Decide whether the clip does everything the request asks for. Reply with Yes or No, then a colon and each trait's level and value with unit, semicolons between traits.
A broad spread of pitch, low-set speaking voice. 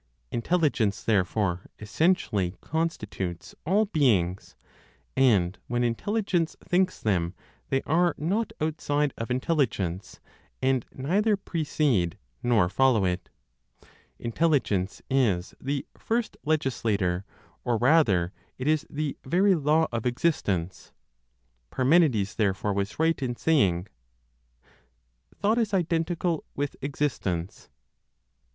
Yes: wide, 8.3 semitones; low, 130 Hz